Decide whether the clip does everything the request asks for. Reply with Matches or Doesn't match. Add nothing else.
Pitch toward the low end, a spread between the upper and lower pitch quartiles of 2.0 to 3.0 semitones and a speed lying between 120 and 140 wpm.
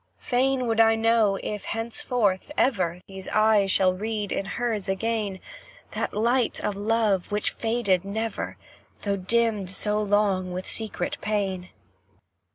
Doesn't match